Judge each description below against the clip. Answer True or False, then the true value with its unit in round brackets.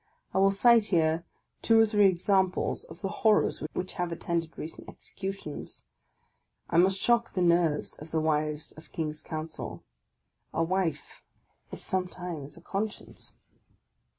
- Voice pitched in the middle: True (175 Hz)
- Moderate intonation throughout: True (3.6 semitones)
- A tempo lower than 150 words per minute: True (140 wpm)